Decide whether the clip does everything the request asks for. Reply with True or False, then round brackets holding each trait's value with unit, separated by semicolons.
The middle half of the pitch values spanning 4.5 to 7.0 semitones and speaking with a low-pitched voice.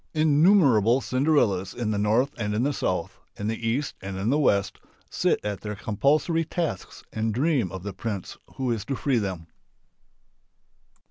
True (5.6 semitones; 115 Hz)